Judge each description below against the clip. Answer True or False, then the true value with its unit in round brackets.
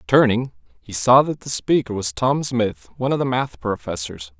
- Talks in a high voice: False (125 Hz)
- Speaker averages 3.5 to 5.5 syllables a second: True (4.9 syllables/s)